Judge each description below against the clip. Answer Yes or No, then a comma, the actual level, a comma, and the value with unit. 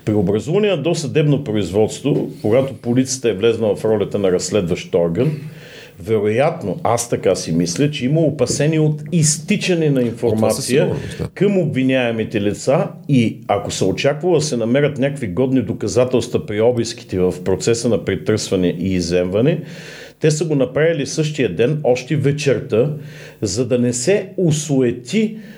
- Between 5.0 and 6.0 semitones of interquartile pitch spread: Yes, average, 5.3 semitones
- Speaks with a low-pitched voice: Yes, low, 130 Hz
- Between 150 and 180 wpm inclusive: No, average, 140 wpm